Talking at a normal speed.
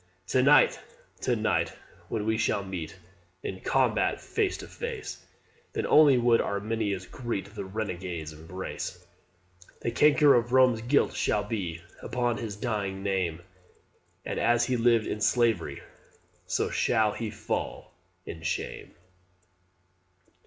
No: slow, 130 wpm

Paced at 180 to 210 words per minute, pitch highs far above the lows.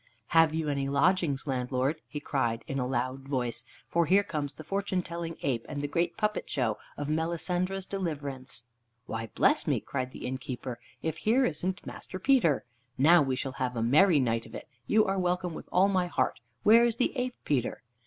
Yes: average, 195 wpm; wide, 5.8 semitones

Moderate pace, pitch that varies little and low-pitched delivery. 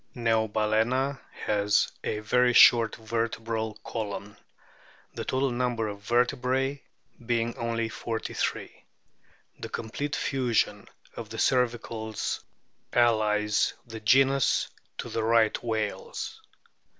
No: slow, 105 wpm; narrow, 2.1 semitones; low, 115 Hz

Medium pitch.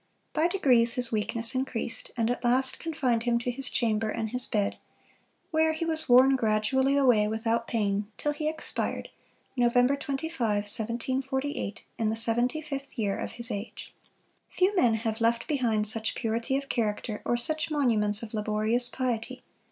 No: high, 240 Hz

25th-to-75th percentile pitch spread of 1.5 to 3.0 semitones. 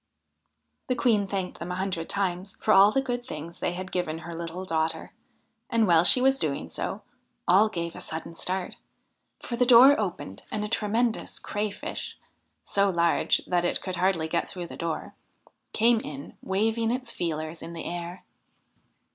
No: average, 4.4 semitones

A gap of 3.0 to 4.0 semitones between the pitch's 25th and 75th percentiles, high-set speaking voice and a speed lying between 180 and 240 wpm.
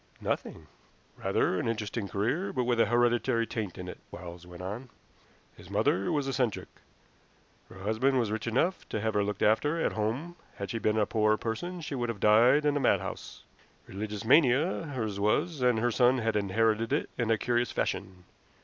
No: average, 3.3 semitones; low, 115 Hz; average, 185 wpm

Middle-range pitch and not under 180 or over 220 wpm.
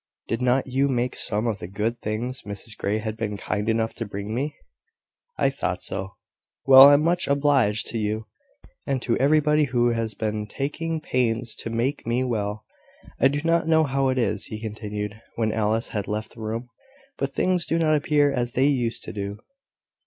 No: low, 120 Hz; average, 190 wpm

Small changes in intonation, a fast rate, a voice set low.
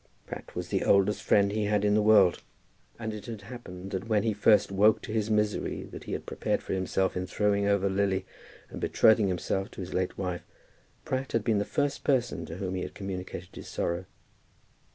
Yes: narrow, 2.3 semitones; fast, 210 wpm; low, 100 Hz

